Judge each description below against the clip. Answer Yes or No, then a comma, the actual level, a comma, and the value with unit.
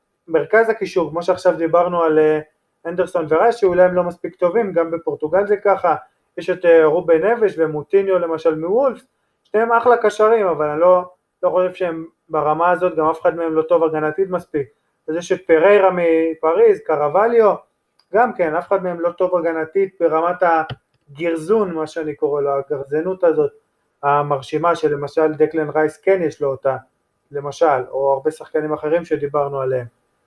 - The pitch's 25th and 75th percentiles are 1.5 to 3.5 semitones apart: Yes, average, 3.1 semitones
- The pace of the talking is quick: Yes, fast, 155 wpm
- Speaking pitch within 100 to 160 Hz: No, medium, 170 Hz